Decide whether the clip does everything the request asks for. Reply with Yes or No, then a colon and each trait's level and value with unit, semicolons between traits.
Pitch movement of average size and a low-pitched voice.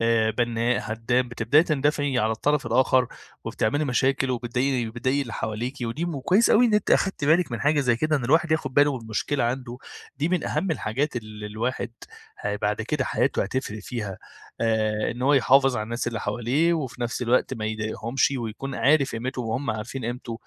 Yes: average, 3.8 semitones; low, 125 Hz